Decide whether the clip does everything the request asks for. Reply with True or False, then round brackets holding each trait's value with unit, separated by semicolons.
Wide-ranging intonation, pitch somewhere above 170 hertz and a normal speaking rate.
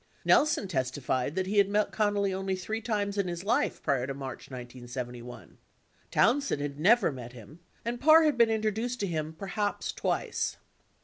True (8.2 semitones; 190 Hz; 175 wpm)